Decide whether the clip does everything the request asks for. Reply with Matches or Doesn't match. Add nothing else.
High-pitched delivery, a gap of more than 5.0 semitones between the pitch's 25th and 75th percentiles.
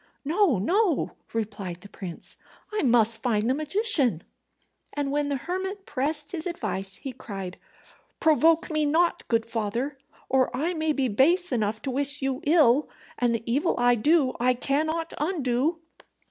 Matches